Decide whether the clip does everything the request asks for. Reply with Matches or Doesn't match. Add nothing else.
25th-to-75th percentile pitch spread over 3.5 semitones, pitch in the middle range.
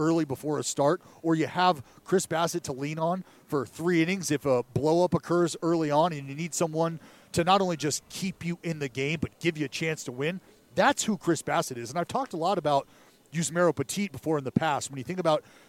Doesn't match